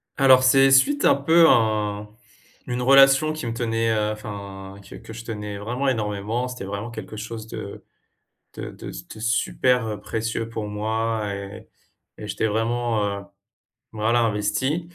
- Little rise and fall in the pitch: No, average, 3.1 semitones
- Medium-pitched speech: No, low, 115 Hz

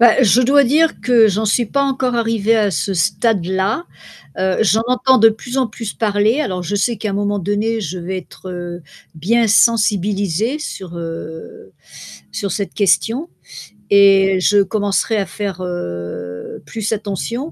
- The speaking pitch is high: Yes, high, 205 Hz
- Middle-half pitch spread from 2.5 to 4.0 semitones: Yes, average, 3.5 semitones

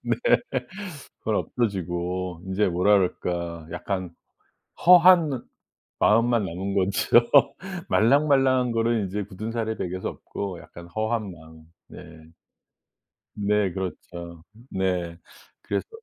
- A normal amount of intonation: Yes, average, 4.5 semitones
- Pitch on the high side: No, very low, 95 Hz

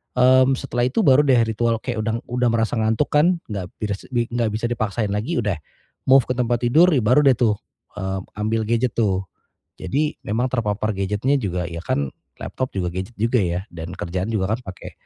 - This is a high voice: No, low, 115 Hz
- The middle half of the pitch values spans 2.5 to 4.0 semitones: Yes, average, 3.7 semitones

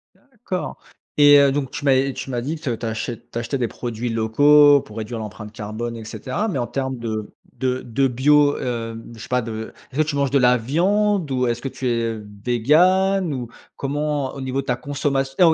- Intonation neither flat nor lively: Yes, average, 3.7 semitones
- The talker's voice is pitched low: Yes, low, 130 Hz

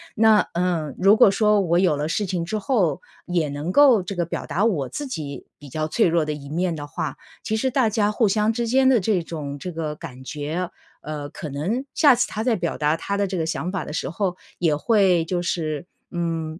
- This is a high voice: No, medium, 175 Hz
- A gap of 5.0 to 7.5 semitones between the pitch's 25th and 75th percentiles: Yes, average, 5.3 semitones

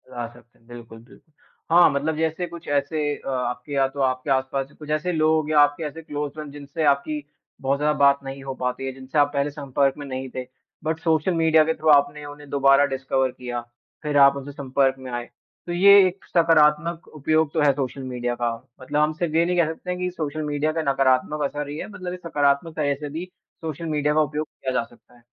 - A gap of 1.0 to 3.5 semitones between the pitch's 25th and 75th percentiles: Yes, average, 2.7 semitones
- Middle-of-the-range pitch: Yes, medium, 145 Hz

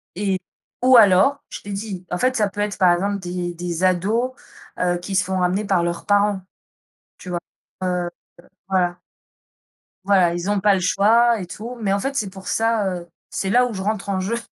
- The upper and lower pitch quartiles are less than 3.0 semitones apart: Yes, narrow, 2.5 semitones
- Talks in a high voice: Yes, high, 195 Hz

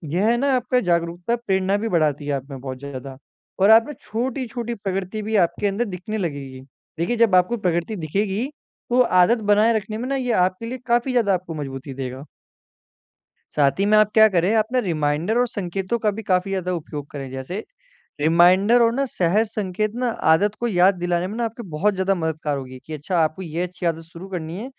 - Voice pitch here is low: No, high, 190 Hz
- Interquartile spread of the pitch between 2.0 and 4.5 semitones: No, wide, 5.4 semitones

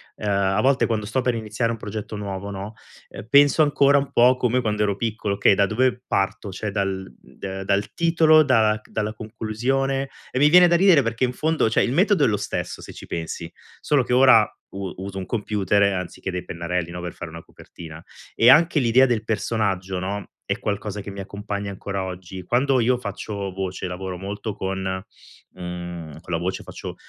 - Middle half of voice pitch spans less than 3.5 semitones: No, average, 4.7 semitones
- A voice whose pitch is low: Yes, low, 105 Hz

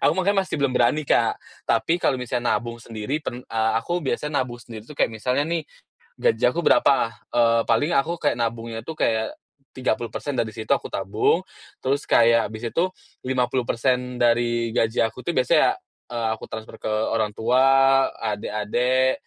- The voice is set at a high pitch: No, low, 120 Hz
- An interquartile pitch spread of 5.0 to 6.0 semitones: No, average, 2.9 semitones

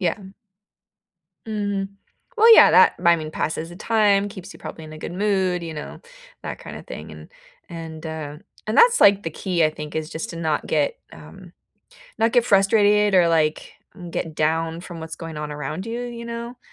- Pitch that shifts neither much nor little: Yes, average, 4.6 semitones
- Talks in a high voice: No, medium, 175 Hz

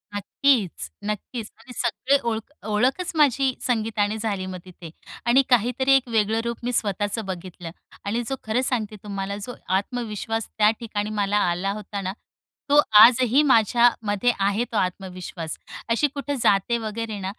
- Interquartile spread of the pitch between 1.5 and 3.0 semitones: No, average, 3.5 semitones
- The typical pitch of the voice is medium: No, high, 220 Hz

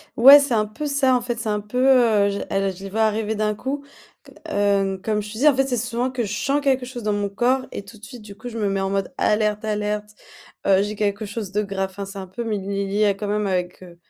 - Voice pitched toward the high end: Yes, high, 210 Hz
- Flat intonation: No, average, 3.1 semitones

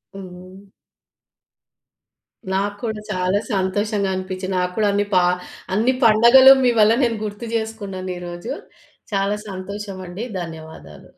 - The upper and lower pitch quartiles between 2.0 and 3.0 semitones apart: Yes, narrow, 2.6 semitones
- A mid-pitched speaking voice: No, high, 200 Hz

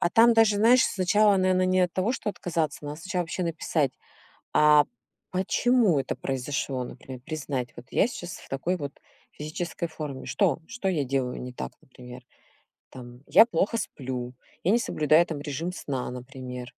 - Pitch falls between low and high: Yes, medium, 155 Hz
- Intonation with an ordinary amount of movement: No, wide, 6.0 semitones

